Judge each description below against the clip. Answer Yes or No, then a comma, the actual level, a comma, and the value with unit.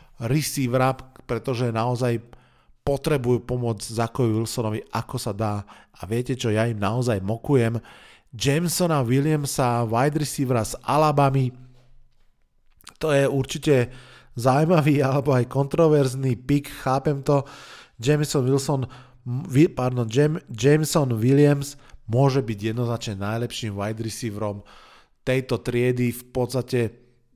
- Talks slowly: Yes, slow, 105 wpm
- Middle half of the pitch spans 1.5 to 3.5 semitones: Yes, average, 3.1 semitones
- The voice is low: Yes, low, 125 Hz